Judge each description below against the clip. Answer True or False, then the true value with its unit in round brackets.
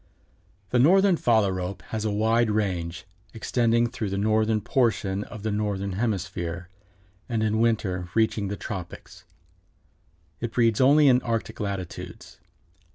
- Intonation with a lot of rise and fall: False (3.1 semitones)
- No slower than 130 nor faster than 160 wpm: True (135 wpm)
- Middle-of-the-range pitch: False (110 Hz)